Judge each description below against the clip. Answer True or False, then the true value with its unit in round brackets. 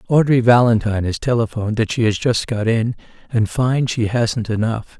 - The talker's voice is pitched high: False (115 Hz)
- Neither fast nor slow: True (180 wpm)